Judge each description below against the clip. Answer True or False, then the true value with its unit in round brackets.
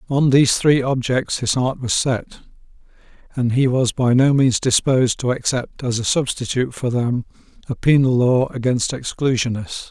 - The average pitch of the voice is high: False (130 Hz)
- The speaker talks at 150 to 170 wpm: True (165 wpm)